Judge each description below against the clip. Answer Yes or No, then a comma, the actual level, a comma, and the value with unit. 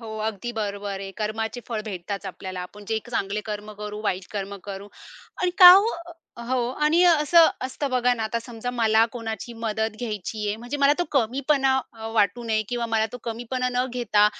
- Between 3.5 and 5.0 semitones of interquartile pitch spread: No, average, 3.0 semitones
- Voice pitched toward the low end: No, high, 225 Hz